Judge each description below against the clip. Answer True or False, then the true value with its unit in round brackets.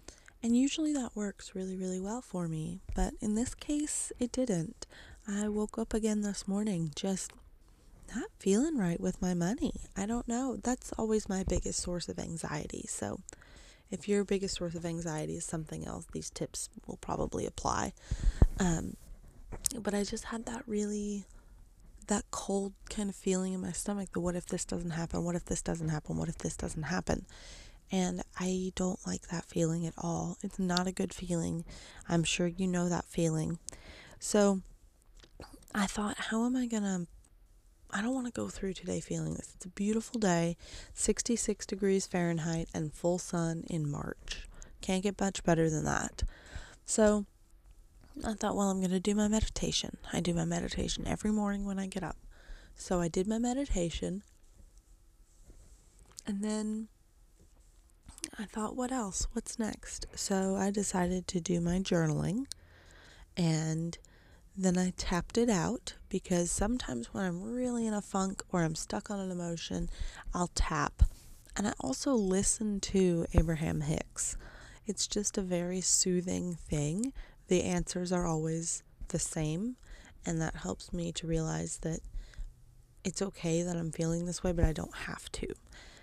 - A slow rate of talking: False (165 wpm)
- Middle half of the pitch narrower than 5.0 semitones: True (3.8 semitones)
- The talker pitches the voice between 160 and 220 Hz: True (185 Hz)